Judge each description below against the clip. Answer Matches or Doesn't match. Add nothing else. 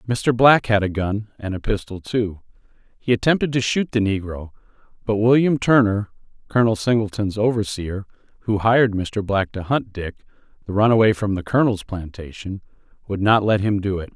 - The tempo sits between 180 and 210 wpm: Doesn't match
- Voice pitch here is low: Matches